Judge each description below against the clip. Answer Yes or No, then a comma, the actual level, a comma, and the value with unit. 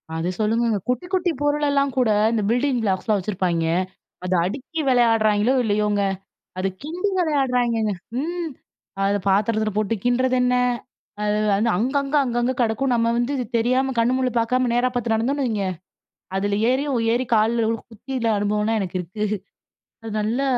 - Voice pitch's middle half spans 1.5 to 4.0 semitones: Yes, average, 3.5 semitones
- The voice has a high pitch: Yes, high, 235 Hz